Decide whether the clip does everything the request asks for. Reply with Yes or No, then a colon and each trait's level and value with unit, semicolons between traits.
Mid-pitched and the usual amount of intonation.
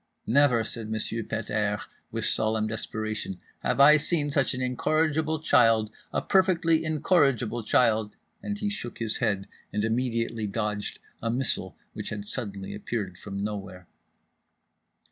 No: low, 115 Hz; average, 5.0 semitones